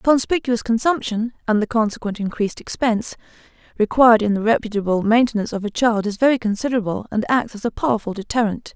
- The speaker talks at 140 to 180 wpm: Yes, average, 170 wpm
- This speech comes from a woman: Yes, female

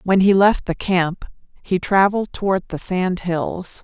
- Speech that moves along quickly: No, average, 170 wpm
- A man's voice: No, female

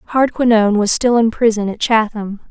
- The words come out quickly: No, average, 170 wpm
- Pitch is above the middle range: Yes, high, 220 Hz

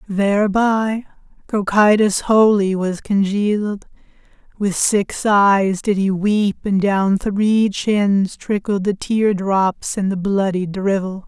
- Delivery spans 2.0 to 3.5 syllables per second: Yes, 3.4 syllables/s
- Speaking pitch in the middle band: No, high, 200 Hz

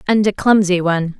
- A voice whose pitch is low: No, high, 190 Hz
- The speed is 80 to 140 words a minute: No, average, 200 wpm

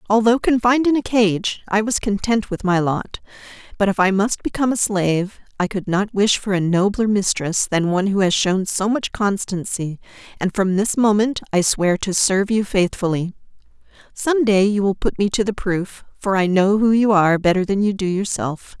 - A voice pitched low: No, high, 200 Hz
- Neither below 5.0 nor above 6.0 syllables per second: Yes, 5.1 syllables/s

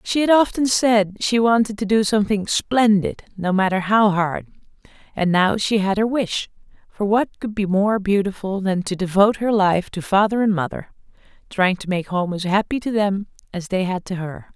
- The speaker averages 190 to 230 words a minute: Yes, average, 200 wpm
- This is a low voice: No, high, 200 Hz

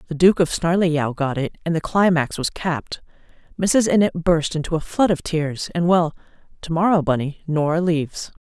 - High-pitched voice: No, medium, 165 Hz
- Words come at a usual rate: Yes, average, 180 wpm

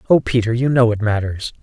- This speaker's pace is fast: Yes, fast, 220 wpm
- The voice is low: Yes, low, 115 Hz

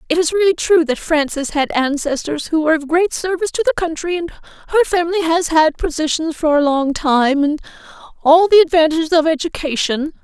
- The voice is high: Yes, very high, 320 Hz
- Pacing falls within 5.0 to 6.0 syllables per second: Yes, 5.8 syllables/s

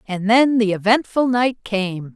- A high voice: Yes, high, 220 Hz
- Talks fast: No, average, 165 wpm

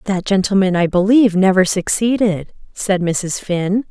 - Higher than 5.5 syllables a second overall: No, 4.5 syllables/s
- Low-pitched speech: No, high, 195 Hz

